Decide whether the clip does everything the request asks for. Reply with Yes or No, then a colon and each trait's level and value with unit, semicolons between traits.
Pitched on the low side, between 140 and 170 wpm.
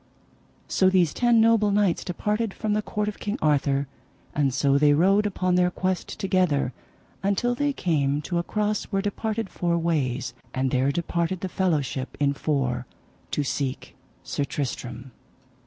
No: medium, 170 Hz; average, 155 wpm